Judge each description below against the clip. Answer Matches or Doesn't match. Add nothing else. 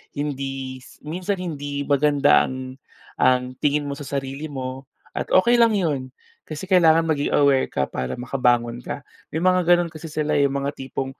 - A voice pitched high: Doesn't match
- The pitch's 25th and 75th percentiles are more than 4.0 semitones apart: Doesn't match